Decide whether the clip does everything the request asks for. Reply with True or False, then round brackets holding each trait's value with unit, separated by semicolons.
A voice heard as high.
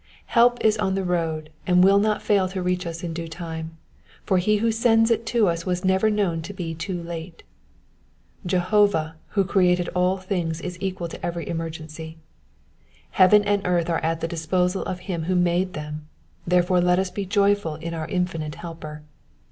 False (180 Hz)